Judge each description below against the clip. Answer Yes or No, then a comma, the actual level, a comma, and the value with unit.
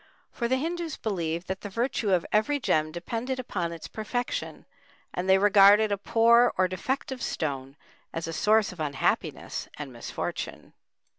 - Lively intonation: Yes, wide, 5.8 semitones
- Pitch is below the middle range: No, high, 200 Hz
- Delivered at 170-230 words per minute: No, average, 155 wpm